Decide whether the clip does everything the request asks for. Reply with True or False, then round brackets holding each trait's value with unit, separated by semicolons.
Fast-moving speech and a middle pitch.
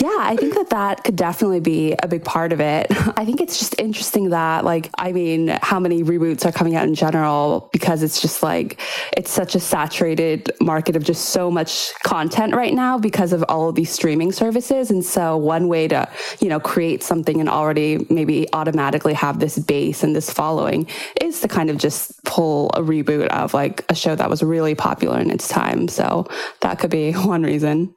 True (210 wpm; 165 Hz)